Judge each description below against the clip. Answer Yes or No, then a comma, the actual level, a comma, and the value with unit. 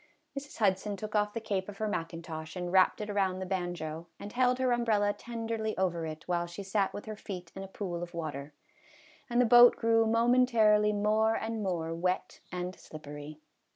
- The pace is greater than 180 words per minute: Yes, average, 190 wpm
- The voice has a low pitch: No, high, 200 Hz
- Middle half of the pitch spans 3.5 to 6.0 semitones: Yes, average, 4.1 semitones